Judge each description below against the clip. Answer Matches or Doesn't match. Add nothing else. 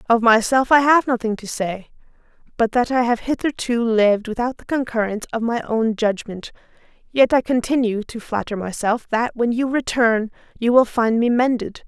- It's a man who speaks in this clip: Doesn't match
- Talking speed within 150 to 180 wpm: Matches